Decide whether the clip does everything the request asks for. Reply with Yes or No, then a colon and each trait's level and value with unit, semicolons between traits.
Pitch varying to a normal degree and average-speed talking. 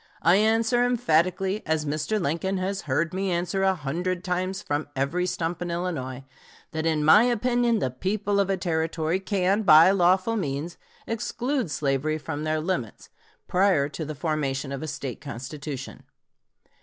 Yes: average, 4.2 semitones; average, 155 wpm